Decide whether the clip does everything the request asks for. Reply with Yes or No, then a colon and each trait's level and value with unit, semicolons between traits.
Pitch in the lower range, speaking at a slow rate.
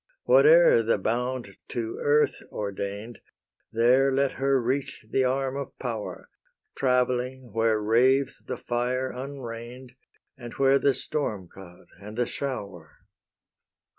Yes: low, 125 Hz; slow, 120 wpm